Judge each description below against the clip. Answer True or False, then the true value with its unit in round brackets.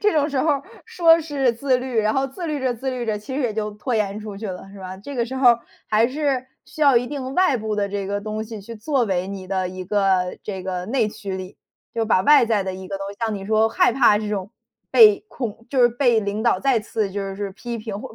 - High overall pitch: True (220 Hz)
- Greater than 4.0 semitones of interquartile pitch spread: True (4.5 semitones)